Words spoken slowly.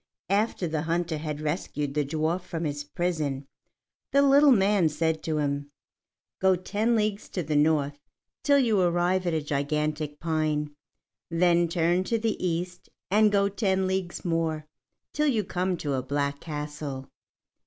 No: average, 155 wpm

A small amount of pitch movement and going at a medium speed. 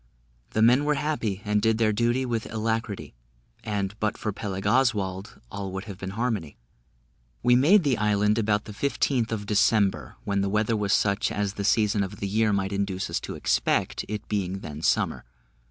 Yes: narrow, 2.2 semitones; average, 185 wpm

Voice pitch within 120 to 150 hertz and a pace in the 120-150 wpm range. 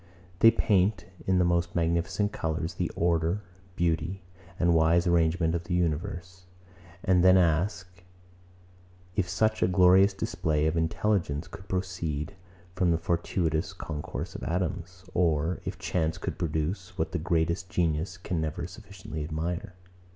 No: very low, 85 Hz; average, 140 wpm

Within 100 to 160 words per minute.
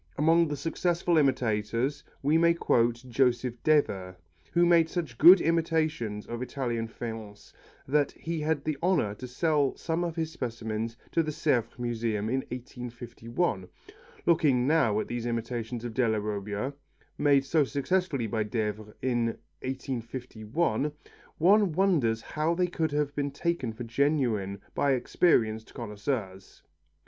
Yes: slow, 135 wpm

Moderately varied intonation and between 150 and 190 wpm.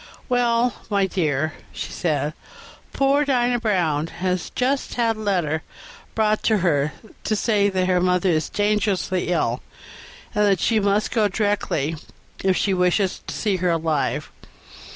No: average, 3.9 semitones; average, 140 wpm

